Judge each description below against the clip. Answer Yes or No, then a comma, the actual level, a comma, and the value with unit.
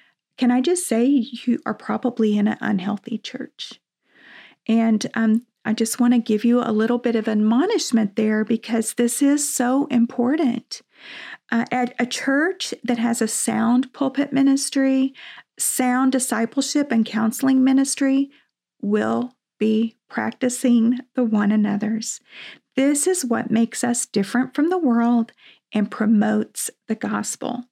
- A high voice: Yes, high, 240 Hz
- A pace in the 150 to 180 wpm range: No, average, 140 wpm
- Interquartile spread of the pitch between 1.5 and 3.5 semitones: Yes, average, 2.9 semitones